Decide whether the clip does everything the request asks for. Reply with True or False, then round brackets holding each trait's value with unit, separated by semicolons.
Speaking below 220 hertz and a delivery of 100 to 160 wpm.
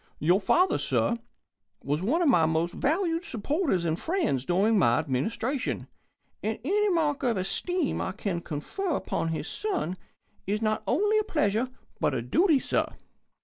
False (225 Hz; 155 wpm)